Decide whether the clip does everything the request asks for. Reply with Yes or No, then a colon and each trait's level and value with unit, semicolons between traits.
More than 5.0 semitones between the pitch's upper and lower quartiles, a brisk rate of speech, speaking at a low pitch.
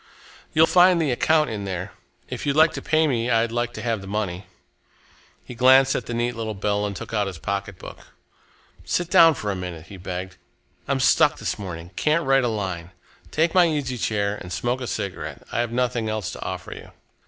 Yes: wide, 5.4 semitones; fast, 210 wpm; low, 115 Hz